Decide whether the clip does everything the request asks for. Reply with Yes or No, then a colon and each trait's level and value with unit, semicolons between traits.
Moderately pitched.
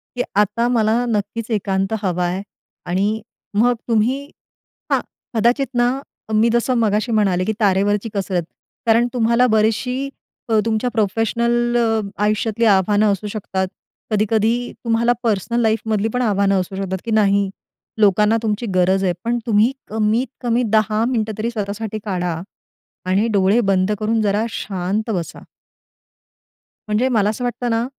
No: high, 215 Hz